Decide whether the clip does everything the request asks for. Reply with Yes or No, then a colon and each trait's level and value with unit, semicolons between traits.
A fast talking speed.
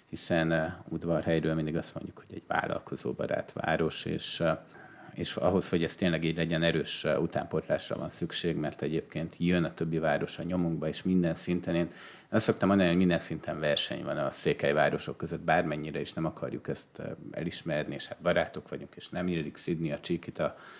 Yes: fast, 180 wpm